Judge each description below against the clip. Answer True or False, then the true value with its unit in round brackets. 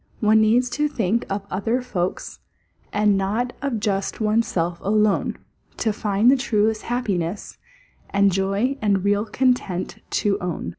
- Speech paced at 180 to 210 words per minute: False (145 wpm)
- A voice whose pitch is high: True (210 Hz)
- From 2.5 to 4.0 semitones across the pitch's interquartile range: True (3.1 semitones)